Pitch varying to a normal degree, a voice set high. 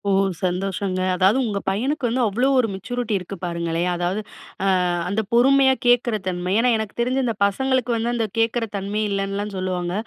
Yes: average, 4.4 semitones; high, 210 Hz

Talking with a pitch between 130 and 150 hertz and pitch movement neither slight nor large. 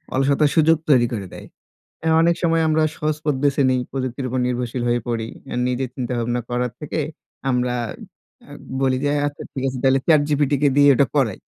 Yes: low, 135 Hz; average, 3.0 semitones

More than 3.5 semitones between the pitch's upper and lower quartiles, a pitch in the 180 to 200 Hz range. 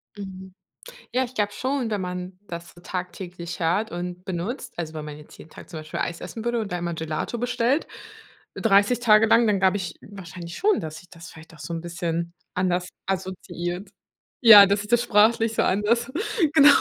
Yes: average, 4.4 semitones; medium, 185 Hz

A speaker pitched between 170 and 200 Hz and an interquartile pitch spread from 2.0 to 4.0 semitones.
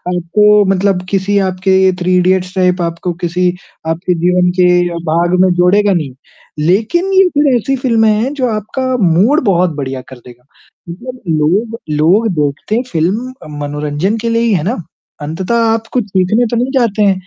No: high, 190 Hz; average, 4.6 semitones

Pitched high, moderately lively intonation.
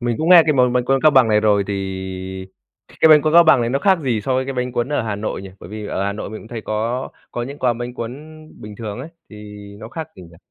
No: low, 120 Hz; average, 4.0 semitones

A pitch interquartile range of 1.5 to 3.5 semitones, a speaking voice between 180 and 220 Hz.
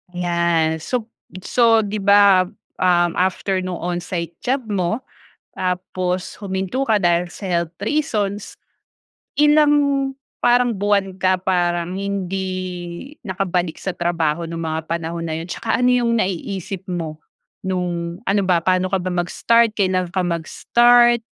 Yes: average, 3.2 semitones; medium, 185 Hz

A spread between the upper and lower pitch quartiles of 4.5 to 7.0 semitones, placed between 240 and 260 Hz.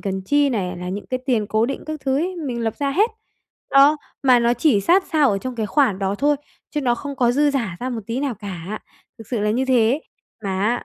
Yes: average, 5.1 semitones; high, 245 Hz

